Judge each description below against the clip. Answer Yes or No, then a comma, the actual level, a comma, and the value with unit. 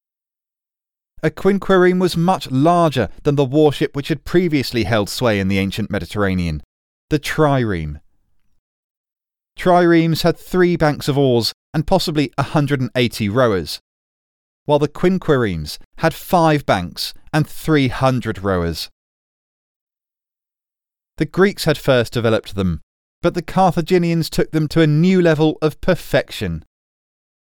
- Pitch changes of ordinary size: No, wide, 8.4 semitones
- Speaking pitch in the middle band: Yes, medium, 145 Hz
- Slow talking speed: Yes, slow, 120 wpm